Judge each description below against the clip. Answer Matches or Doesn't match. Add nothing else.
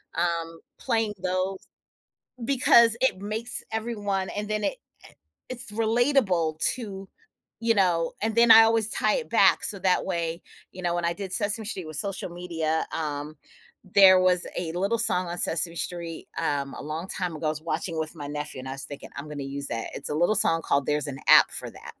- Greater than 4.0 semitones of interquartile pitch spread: Matches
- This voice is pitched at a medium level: Matches